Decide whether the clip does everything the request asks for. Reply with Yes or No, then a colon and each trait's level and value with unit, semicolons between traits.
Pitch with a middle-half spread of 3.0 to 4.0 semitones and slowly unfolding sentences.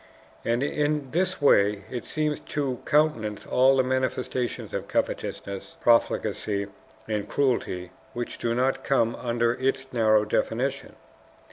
Yes: average, 3.4 semitones; slow, 125 wpm